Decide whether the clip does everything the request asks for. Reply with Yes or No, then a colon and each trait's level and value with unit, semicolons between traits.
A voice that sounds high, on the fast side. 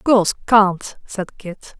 No: high, 200 Hz; slow, 135 wpm